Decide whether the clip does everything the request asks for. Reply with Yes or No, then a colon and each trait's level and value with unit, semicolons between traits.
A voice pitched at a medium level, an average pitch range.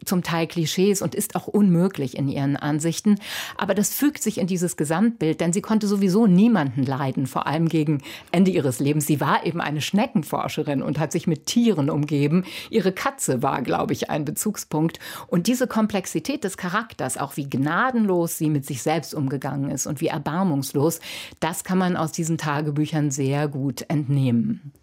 Yes: medium, 165 Hz; average, 4.9 semitones